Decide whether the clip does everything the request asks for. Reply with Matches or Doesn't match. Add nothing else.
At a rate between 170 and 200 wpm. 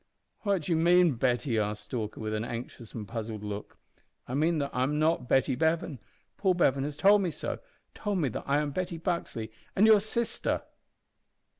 Matches